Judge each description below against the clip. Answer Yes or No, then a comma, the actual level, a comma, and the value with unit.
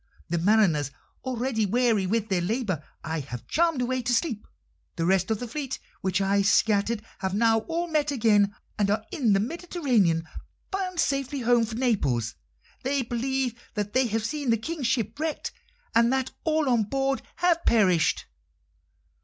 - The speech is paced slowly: No, average, 165 wpm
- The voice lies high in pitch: Yes, high, 230 Hz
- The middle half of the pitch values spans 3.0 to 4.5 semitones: No, average, 5.1 semitones